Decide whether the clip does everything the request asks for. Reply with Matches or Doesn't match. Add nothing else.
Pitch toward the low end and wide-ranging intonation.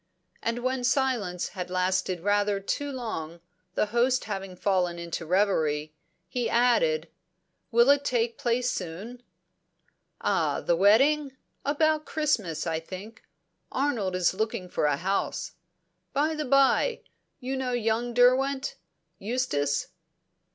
Doesn't match